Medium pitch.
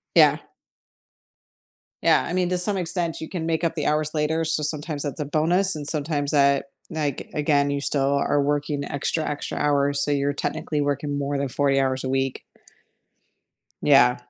Yes: medium, 145 Hz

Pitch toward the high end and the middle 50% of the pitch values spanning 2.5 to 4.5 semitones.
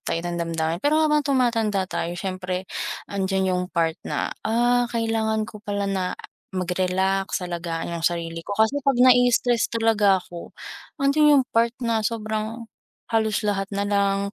Yes: high, 205 Hz; average, 4.0 semitones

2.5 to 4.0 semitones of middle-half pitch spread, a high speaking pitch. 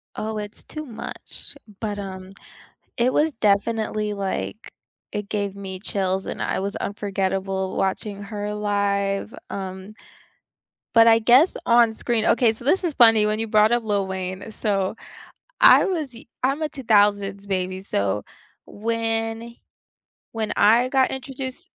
Yes: average, 2.8 semitones; high, 210 Hz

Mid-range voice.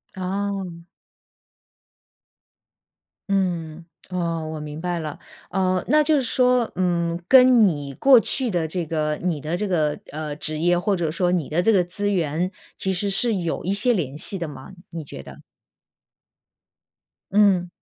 Yes: medium, 175 Hz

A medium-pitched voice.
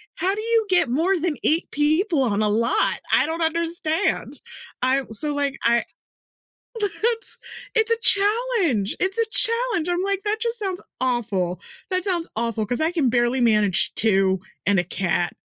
No: very high, 320 Hz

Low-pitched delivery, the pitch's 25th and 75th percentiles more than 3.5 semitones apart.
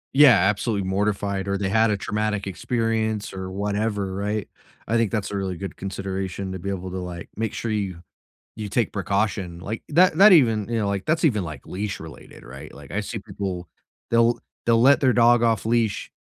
No: low, 105 Hz; average, 2.9 semitones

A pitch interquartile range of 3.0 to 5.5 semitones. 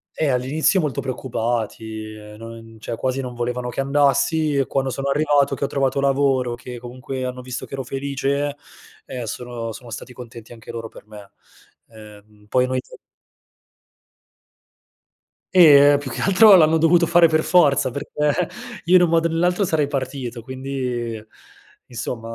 Yes: average, 3.3 semitones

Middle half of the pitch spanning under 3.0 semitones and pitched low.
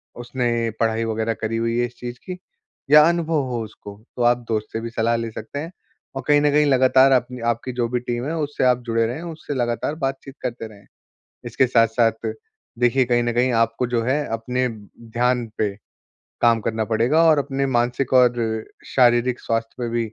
Yes: narrow, 2.6 semitones; low, 120 Hz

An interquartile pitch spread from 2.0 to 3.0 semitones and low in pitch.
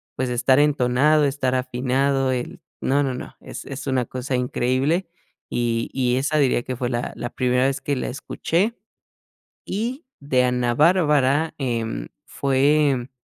Yes: narrow, 2.5 semitones; low, 130 Hz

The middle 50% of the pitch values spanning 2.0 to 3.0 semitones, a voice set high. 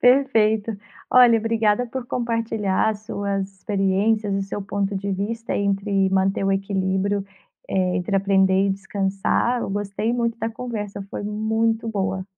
Yes: narrow, 2.5 semitones; high, 205 Hz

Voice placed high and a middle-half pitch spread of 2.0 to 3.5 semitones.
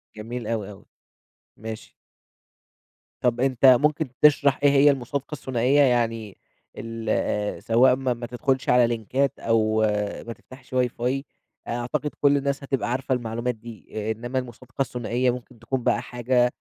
No: low, 125 Hz; narrow, 2.5 semitones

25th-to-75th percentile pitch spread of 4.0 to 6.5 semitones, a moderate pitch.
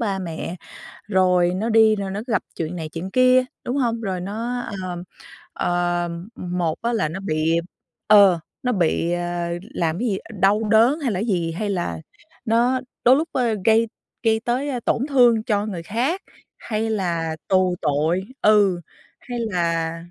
No: average, 4.7 semitones; high, 200 Hz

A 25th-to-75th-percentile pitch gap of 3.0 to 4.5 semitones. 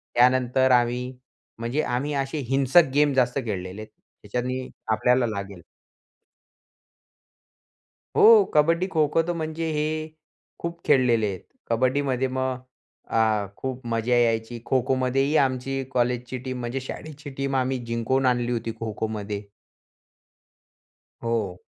No: narrow, 2.6 semitones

